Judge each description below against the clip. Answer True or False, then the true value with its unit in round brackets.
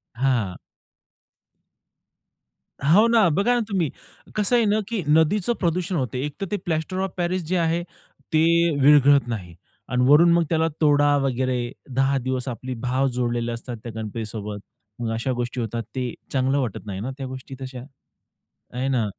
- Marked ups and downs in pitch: True (5.8 semitones)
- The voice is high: False (135 Hz)